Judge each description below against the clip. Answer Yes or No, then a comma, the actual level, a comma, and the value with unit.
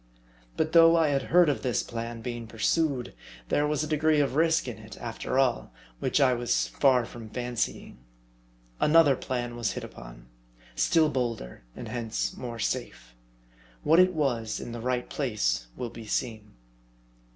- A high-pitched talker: No, low, 125 Hz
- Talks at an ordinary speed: Yes, average, 160 wpm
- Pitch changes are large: No, average, 4.6 semitones